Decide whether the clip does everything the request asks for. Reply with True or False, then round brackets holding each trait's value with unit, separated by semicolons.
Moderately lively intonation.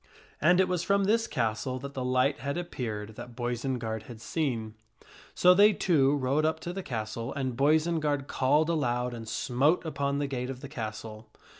True (4.6 semitones)